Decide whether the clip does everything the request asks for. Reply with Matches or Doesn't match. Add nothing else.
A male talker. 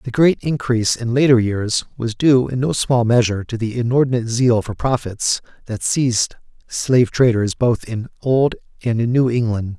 Matches